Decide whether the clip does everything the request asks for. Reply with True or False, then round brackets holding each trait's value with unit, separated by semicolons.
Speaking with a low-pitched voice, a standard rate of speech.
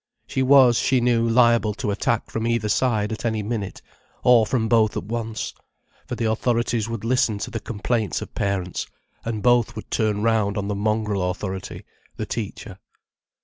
True (110 Hz; 175 wpm)